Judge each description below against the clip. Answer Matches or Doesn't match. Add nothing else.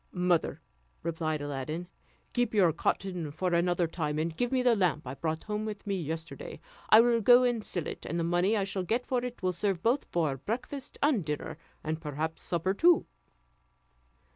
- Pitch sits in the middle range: Matches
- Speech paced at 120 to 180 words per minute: Doesn't match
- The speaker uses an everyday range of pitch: Doesn't match